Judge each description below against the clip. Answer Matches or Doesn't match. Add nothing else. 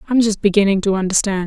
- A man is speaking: Doesn't match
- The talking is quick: Matches